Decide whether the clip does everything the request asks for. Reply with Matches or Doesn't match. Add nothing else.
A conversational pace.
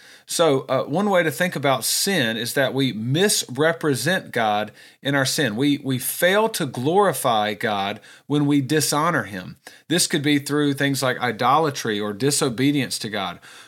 Matches